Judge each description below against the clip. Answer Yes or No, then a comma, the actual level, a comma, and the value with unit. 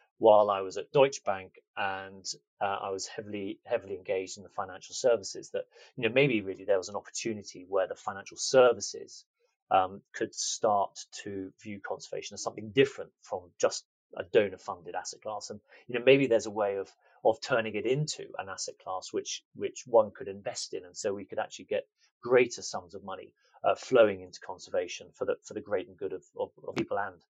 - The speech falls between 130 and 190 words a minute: No, average, 200 wpm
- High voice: Yes, very high, 395 Hz